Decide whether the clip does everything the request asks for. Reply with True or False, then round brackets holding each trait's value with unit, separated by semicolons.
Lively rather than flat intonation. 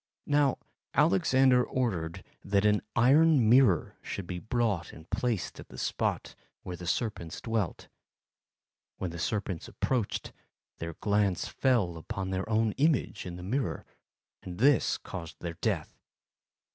True (5.8 semitones)